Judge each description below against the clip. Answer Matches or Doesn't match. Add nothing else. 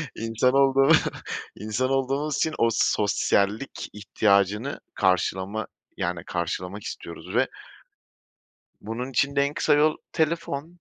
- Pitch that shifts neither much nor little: Doesn't match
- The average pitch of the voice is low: Matches